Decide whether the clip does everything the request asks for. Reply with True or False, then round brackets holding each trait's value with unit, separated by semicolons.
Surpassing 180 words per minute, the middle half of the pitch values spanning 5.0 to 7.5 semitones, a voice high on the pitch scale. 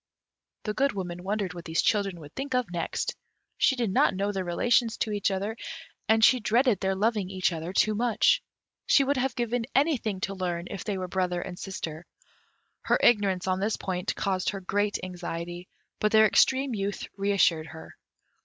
False (190 wpm; 3.6 semitones; 195 Hz)